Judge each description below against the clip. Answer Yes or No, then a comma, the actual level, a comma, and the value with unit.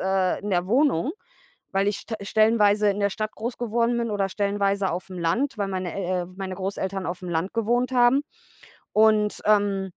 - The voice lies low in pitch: No, high, 200 Hz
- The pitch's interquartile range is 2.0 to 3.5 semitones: Yes, narrow, 2.6 semitones